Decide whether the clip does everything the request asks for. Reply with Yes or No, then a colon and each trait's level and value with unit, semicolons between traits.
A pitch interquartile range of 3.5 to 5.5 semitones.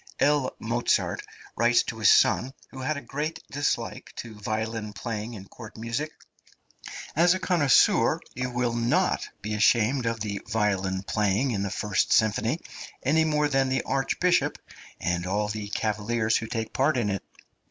Yes: average, 4.1 semitones